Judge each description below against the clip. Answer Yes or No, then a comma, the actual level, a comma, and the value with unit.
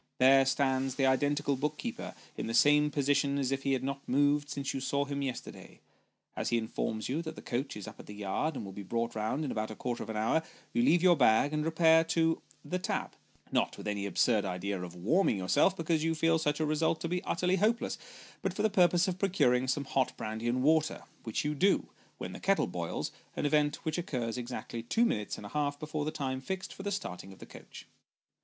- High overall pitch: No, medium, 140 Hz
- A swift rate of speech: Yes, fast, 235 wpm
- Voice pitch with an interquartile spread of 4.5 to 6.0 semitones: Yes, average, 5.3 semitones